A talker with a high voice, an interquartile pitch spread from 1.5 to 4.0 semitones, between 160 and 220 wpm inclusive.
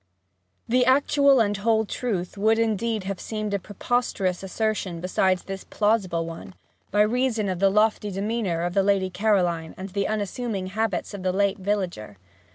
Yes: high, 200 Hz; average, 2.9 semitones; average, 165 wpm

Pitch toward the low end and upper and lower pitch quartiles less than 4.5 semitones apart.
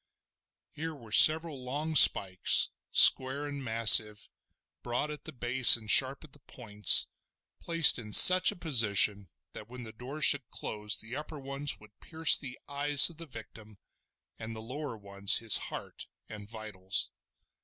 No: low, 125 Hz; average, 5.3 semitones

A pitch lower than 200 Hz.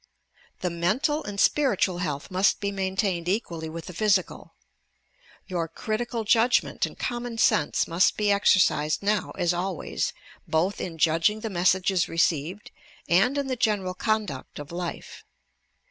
Yes: high, 190 Hz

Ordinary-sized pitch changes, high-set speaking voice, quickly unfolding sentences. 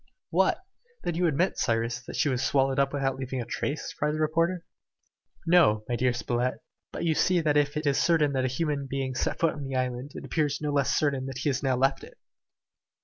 No: average, 3.0 semitones; medium, 140 Hz; fast, 225 wpm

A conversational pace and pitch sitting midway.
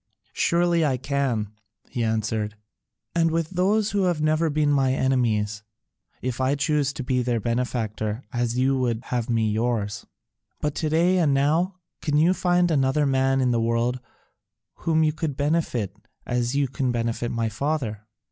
No: average, 165 wpm; low, 130 Hz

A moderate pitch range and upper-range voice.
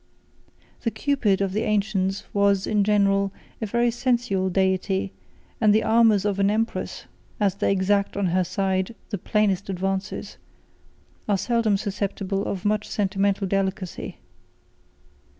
No: narrow, 1.7 semitones; high, 200 Hz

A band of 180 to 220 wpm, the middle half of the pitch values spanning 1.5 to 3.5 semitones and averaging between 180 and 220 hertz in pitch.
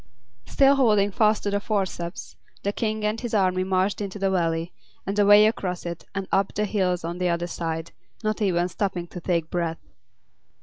Yes: average, 185 wpm; average, 3.1 semitones; high, 190 Hz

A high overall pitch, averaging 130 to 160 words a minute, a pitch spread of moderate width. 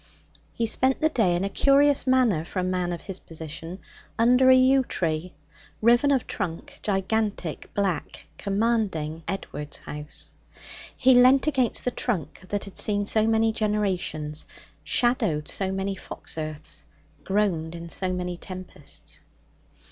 No: high, 195 Hz; average, 140 wpm; wide, 5.9 semitones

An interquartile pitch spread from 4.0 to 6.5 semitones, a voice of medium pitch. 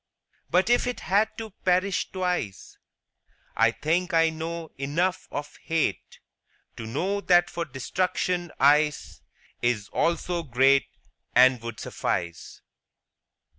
Yes: wide, 5.5 semitones; medium, 165 Hz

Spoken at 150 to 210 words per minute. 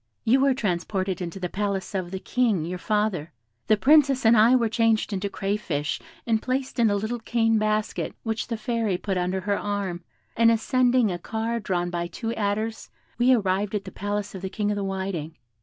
Yes: average, 200 wpm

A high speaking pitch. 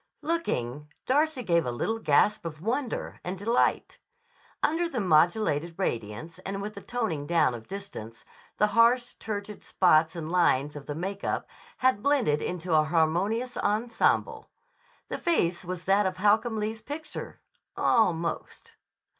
Yes: high, 195 Hz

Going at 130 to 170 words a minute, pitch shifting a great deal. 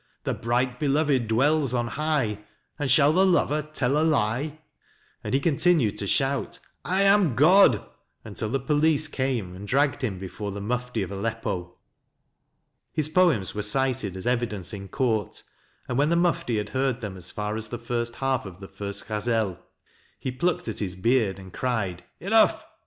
No: average, 180 wpm; wide, 5.8 semitones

